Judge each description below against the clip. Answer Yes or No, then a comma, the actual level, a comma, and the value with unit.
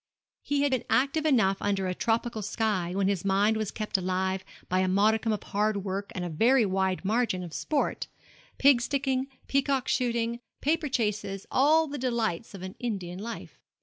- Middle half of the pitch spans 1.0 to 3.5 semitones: No, average, 5.0 semitones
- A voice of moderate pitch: No, high, 215 Hz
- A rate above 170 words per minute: Yes, average, 180 wpm